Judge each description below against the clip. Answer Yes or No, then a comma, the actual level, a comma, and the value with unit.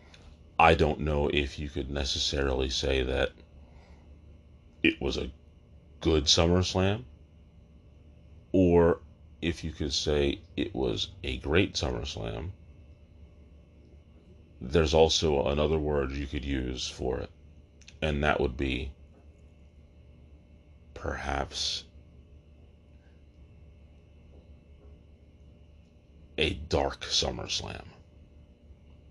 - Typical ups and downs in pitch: No, narrow, 1.8 semitones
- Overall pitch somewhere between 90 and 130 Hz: No, very low, 80 Hz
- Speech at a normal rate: No, slow, 90 wpm